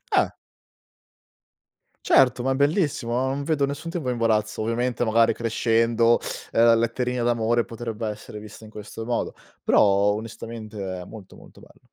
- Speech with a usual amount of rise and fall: No, narrow, 2.1 semitones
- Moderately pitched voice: No, low, 115 Hz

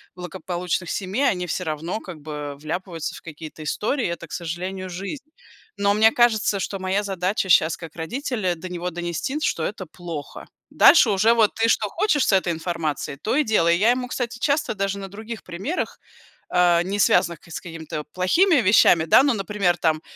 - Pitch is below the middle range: No, medium, 185 Hz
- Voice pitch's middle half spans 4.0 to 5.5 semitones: Yes, average, 4.3 semitones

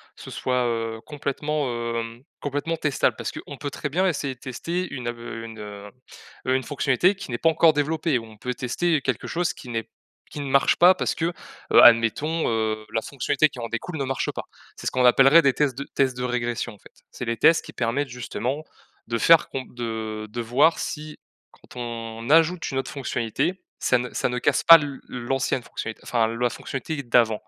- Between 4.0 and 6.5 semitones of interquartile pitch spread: Yes, average, 4.3 semitones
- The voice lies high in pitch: No, low, 130 Hz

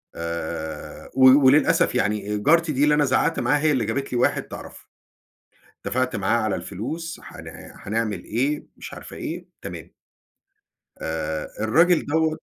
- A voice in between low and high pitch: No, low, 125 Hz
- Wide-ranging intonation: Yes, wide, 6.3 semitones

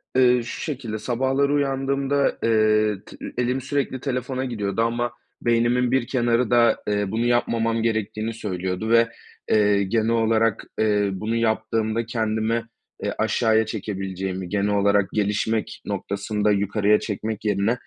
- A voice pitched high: No, low, 110 Hz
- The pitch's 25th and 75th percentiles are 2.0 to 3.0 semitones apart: Yes, narrow, 2.6 semitones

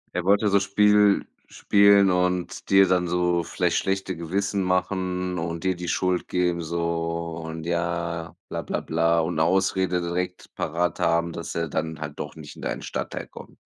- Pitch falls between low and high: No, very low, 90 Hz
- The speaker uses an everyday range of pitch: No, narrow, 2.0 semitones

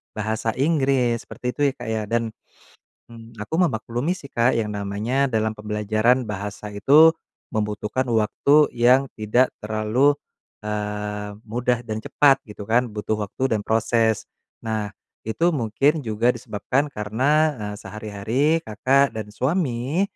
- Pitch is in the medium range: No, low, 115 Hz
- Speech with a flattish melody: No, average, 3.6 semitones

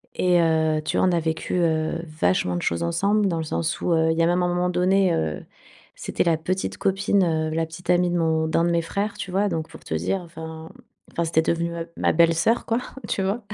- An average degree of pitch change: No, narrow, 2.0 semitones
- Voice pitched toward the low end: No, medium, 170 Hz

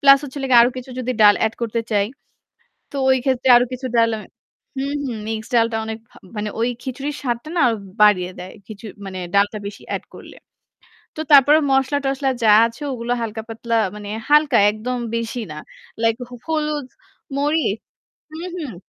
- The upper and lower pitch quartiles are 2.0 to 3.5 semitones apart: No, average, 3.9 semitones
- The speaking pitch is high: Yes, high, 240 Hz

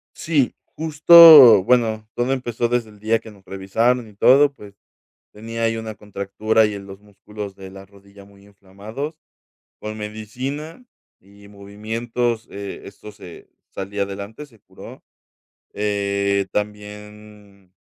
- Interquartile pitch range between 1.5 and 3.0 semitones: Yes, average, 2.7 semitones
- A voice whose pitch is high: No, low, 105 Hz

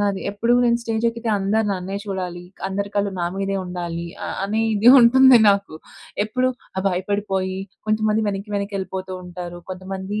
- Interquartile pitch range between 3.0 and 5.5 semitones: No, narrow, 2.5 semitones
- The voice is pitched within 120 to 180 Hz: No, high, 200 Hz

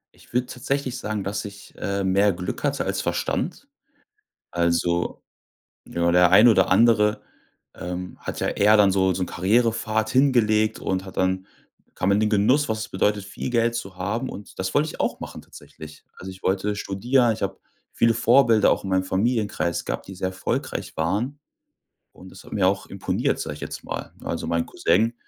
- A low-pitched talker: Yes, low, 100 Hz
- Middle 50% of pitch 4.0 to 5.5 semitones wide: No, average, 3.4 semitones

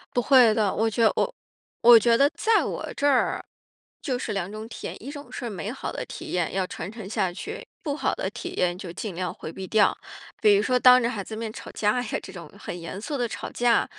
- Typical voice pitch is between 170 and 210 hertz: No, high, 220 Hz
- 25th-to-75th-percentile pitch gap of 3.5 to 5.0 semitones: Yes, average, 4.3 semitones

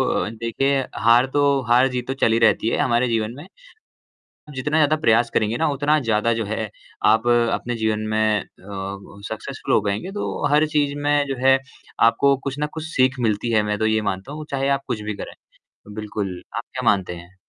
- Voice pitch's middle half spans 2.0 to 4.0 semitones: No, average, 4.5 semitones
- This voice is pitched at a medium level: No, low, 115 Hz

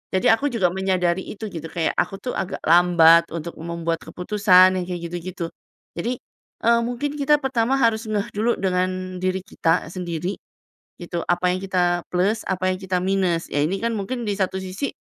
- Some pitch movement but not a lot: Yes, average, 3.1 semitones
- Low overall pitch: No, medium, 185 Hz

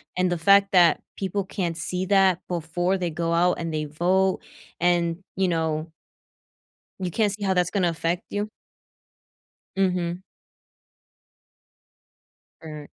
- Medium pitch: Yes, medium, 180 Hz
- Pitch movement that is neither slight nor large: No, narrow, 2.3 semitones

